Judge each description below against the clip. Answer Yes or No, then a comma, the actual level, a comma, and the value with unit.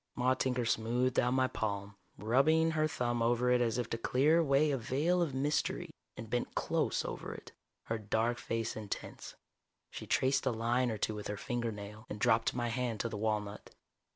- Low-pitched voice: Yes, low, 120 Hz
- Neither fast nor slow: Yes, average, 190 wpm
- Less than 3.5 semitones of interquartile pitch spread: Yes, average, 2.8 semitones